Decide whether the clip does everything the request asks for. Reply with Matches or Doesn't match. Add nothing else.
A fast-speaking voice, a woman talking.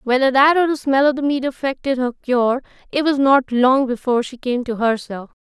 Matches